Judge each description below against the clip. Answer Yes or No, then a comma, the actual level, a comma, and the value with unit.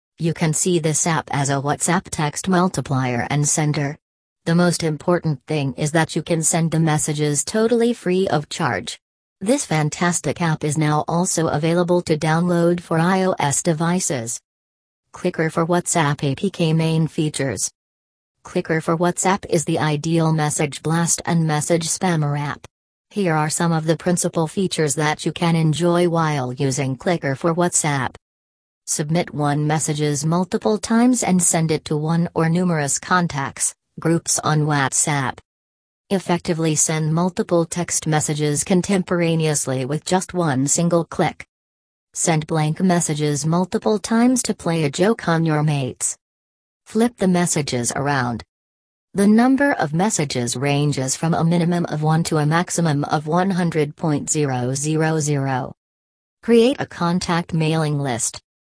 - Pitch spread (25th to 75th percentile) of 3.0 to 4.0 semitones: Yes, average, 3.3 semitones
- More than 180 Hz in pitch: No, medium, 160 Hz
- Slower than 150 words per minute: Yes, average, 140 wpm